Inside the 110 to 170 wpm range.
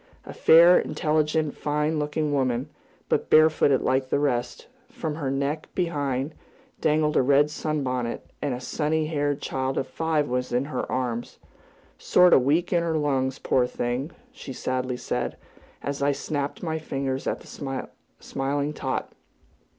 Yes: average, 155 wpm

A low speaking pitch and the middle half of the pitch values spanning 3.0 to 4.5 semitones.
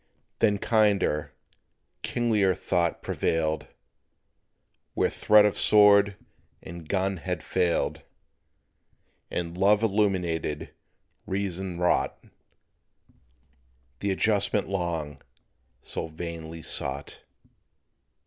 Yes: very low, 95 Hz; average, 3.5 semitones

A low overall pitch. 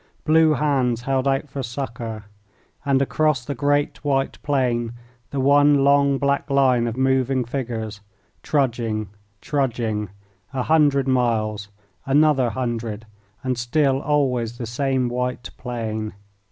Yes: low, 130 Hz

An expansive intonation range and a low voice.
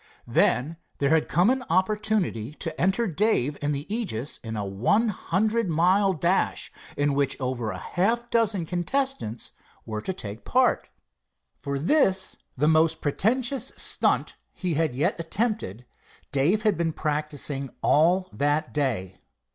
No: wide, 6.8 semitones; medium, 165 Hz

